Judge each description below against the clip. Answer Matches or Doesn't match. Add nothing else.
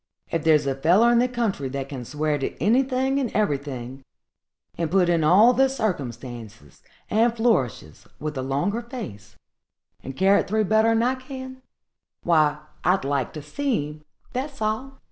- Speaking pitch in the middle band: Matches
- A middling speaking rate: Matches